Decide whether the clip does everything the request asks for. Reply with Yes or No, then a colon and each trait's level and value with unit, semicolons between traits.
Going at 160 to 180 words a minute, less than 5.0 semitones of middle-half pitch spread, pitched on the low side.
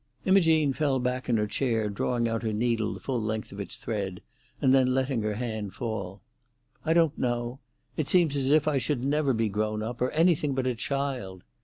No: fast, 205 wpm; average, 4.2 semitones; low, 125 Hz